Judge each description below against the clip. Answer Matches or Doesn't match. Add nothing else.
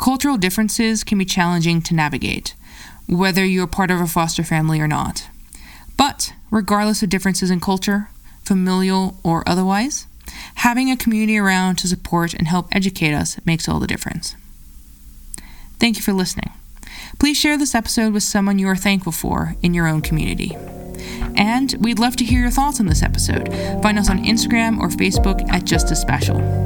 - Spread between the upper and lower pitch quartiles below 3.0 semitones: Doesn't match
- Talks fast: Doesn't match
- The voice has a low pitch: Doesn't match